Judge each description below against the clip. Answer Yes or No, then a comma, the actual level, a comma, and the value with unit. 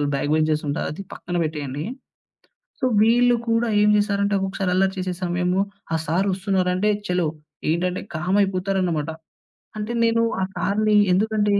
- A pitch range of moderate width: Yes, average, 3.0 semitones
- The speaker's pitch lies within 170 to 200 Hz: Yes, high, 190 Hz